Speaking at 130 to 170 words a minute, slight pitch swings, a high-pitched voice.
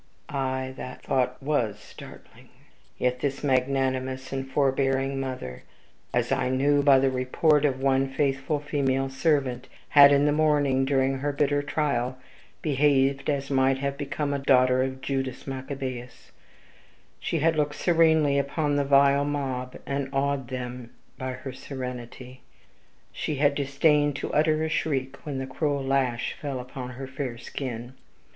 No: average, 150 wpm; narrow, 1.6 semitones; low, 135 Hz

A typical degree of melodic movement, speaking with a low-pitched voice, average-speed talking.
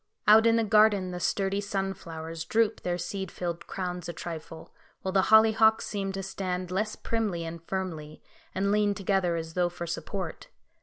No: average, 3.0 semitones; high, 190 Hz; average, 170 wpm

